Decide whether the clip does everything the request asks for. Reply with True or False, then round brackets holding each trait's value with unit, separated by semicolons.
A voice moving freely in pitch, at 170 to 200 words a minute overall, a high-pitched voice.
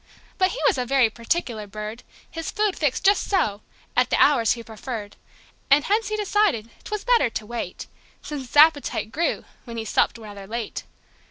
True (8.0 semitones; 180 wpm; 250 Hz)